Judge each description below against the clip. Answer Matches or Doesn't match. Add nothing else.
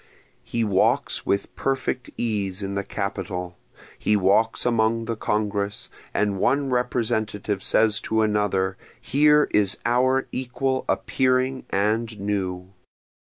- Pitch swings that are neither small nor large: Matches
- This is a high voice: Doesn't match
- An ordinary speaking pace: Doesn't match